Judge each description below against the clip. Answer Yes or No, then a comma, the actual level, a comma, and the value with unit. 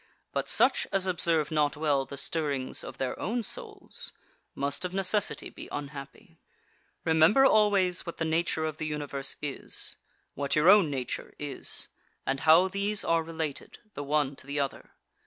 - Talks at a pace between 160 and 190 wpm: Yes, average, 165 wpm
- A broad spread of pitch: No, average, 4.4 semitones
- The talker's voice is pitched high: No, medium, 160 Hz